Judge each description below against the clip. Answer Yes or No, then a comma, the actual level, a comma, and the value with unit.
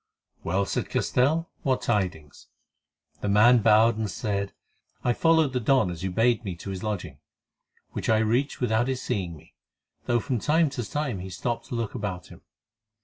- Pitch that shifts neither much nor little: Yes, average, 4.5 semitones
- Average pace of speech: Yes, average, 180 wpm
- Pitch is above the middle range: No, low, 110 Hz